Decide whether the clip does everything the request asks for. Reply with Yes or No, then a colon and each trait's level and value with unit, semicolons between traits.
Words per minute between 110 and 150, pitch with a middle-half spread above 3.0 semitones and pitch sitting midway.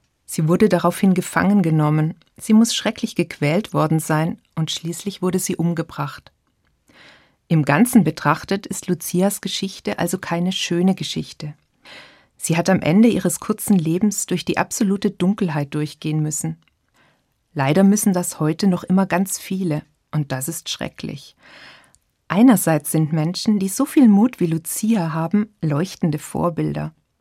Yes: average, 140 wpm; average, 3.8 semitones; medium, 175 Hz